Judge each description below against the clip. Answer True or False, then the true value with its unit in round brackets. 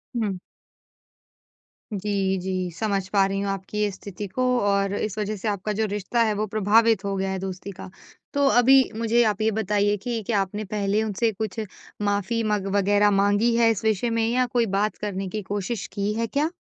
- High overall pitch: True (205 Hz)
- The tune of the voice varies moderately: False (2.1 semitones)